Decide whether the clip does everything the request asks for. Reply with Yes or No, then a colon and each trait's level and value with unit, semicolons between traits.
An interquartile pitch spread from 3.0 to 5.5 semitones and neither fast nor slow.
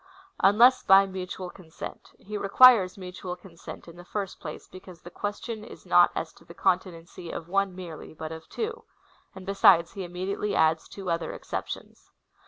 No: narrow, 2.4 semitones; average, 180 wpm